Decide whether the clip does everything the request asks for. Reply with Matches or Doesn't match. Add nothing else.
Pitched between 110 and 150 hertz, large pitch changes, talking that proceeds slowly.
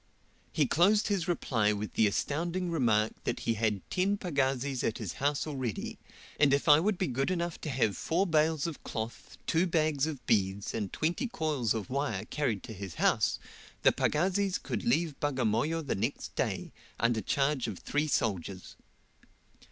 Doesn't match